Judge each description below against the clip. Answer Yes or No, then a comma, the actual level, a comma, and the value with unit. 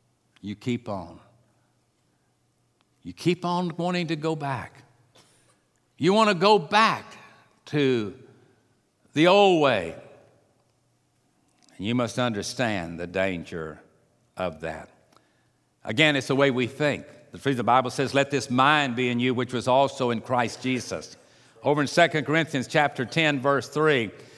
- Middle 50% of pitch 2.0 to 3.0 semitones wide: No, average, 3.9 semitones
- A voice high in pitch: No, low, 130 Hz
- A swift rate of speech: No, average, 145 wpm